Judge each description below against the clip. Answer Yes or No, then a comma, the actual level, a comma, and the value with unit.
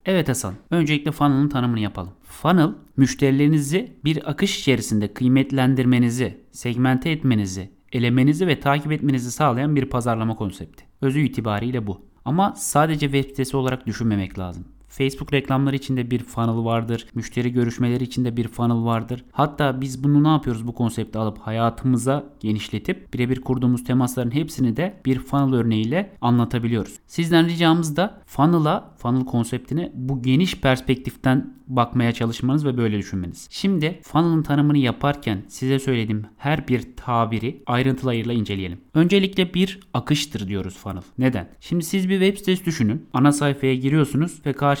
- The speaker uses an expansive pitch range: No, average, 3.8 semitones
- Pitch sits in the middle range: No, low, 130 Hz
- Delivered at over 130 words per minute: Yes, fast, 140 wpm